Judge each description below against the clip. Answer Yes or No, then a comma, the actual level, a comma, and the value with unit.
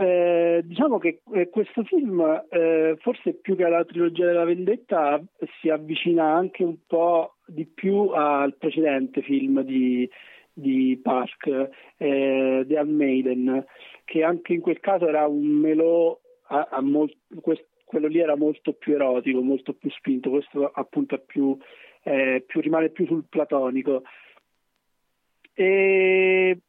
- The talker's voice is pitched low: No, medium, 160 Hz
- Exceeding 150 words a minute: No, average, 130 wpm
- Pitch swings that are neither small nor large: Yes, average, 3.7 semitones